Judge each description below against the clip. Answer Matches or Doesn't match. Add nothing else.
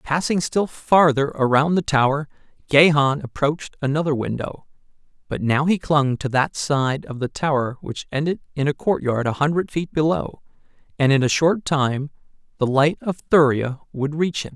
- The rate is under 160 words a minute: Doesn't match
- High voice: Doesn't match